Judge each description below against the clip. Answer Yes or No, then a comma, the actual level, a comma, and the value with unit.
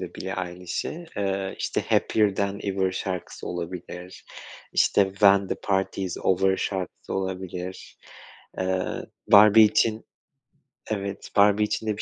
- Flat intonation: Yes, narrow, 1.6 semitones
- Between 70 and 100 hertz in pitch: Yes, very low, 95 Hz